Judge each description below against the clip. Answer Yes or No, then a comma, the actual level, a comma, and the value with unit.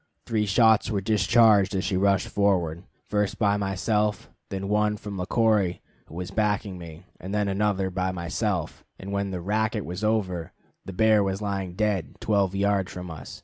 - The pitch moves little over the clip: Yes, narrow, 2.2 semitones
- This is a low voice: Yes, low, 100 Hz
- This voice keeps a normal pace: Yes, average, 180 wpm